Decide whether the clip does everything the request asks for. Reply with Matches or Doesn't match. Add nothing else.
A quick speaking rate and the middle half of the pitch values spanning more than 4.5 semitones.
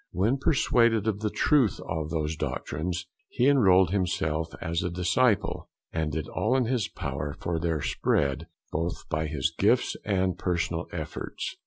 Doesn't match